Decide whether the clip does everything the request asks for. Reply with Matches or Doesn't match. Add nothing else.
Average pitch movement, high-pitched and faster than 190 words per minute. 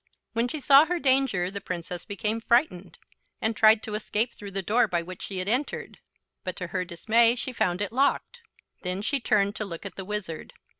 Matches